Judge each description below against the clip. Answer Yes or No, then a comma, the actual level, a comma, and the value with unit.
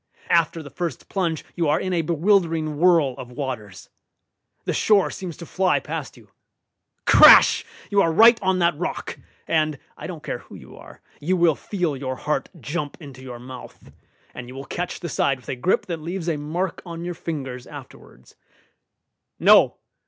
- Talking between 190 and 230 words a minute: No, average, 180 wpm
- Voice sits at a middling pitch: Yes, medium, 165 Hz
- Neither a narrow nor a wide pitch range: Yes, average, 4.1 semitones